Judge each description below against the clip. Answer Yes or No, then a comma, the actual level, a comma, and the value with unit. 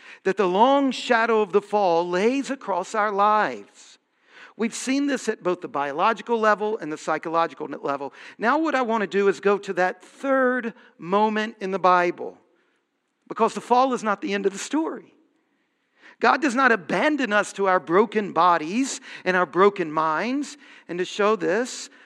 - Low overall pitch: No, high, 210 Hz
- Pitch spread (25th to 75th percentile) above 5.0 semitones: Yes, wide, 5.5 semitones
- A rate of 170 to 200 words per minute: Yes, average, 175 wpm